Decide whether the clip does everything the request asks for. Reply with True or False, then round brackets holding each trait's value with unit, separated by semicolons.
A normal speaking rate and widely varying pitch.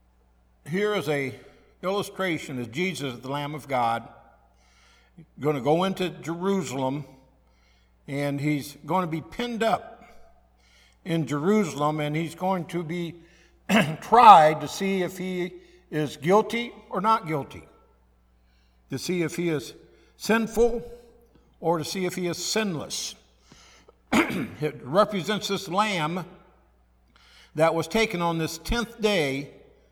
False (125 wpm; 6.2 semitones)